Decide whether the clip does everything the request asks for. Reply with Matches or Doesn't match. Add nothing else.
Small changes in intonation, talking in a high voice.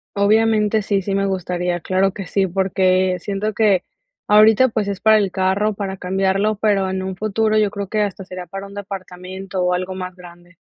Matches